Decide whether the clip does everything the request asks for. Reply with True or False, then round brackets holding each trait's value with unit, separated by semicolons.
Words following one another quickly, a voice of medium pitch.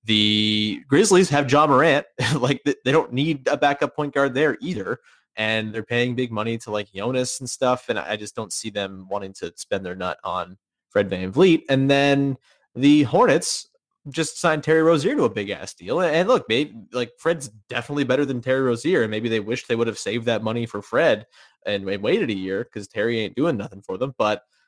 False (215 wpm; 120 Hz)